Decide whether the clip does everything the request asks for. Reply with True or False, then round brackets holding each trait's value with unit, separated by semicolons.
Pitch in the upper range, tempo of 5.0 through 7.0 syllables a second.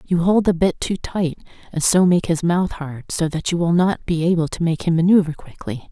False (170 Hz; 5.2 syllables/s)